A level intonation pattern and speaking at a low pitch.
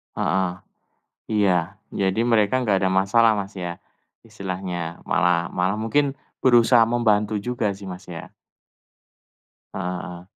No: average, 3.9 semitones; low, 100 Hz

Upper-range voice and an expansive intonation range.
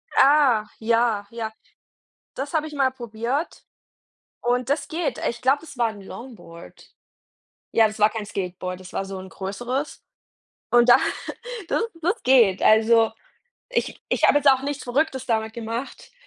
No: high, 235 Hz; average, 3.9 semitones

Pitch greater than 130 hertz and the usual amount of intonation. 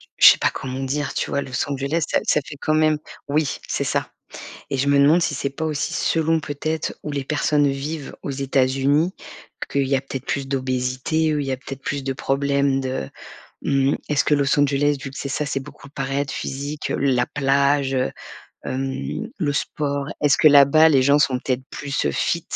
No: medium, 140 Hz; narrow, 1.6 semitones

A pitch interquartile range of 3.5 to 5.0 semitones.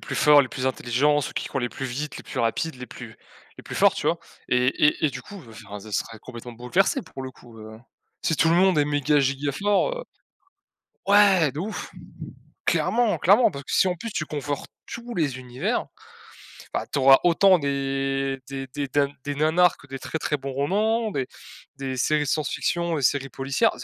Yes: average, 4.6 semitones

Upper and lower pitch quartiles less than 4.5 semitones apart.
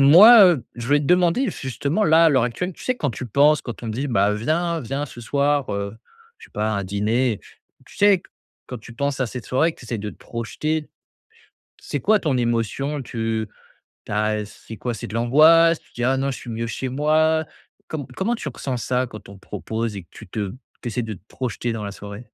No: wide, 5.4 semitones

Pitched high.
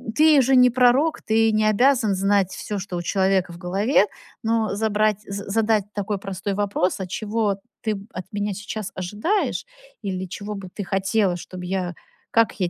Yes: high, 205 Hz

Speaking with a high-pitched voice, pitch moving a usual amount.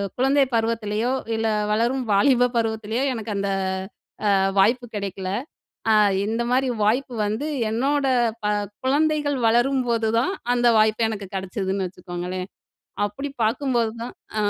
Yes: high, 225 Hz; average, 3.8 semitones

